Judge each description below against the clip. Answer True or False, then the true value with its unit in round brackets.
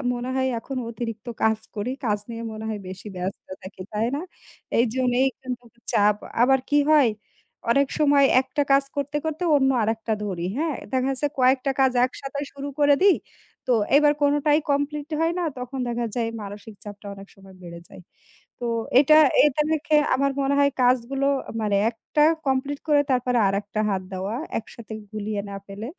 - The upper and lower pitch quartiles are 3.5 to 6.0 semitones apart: True (4.8 semitones)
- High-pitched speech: True (250 Hz)